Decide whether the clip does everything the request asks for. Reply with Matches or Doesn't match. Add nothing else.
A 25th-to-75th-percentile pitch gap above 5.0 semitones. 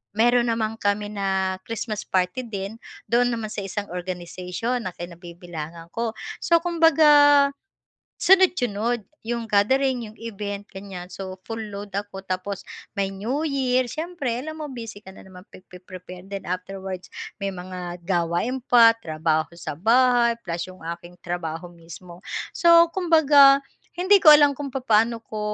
Matches